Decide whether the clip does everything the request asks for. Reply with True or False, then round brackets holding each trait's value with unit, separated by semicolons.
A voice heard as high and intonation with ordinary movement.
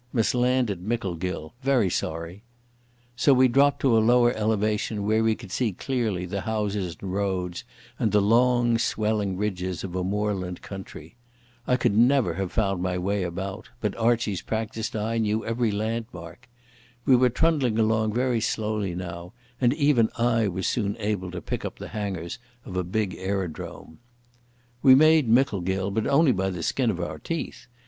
False (105 Hz; 4.1 semitones)